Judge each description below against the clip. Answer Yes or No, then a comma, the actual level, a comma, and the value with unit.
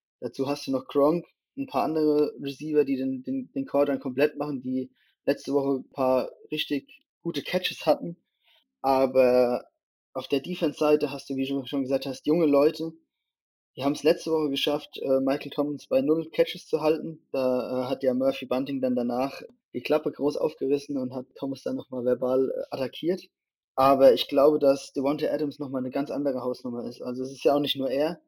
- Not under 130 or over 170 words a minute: No, fast, 190 wpm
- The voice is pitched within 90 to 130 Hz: No, medium, 140 Hz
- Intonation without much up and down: Yes, narrow, 2.3 semitones